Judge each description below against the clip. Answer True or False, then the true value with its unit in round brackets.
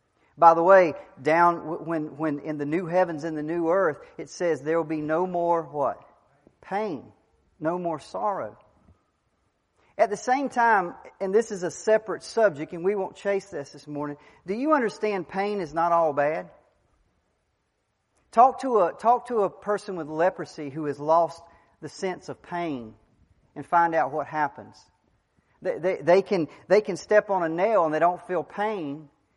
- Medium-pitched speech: True (170 Hz)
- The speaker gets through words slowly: False (180 wpm)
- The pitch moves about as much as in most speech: True (4.0 semitones)